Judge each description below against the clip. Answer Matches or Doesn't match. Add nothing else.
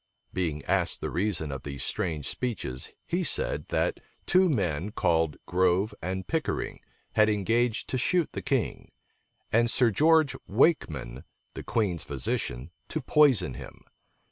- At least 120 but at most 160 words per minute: Matches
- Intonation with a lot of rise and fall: Matches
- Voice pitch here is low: Matches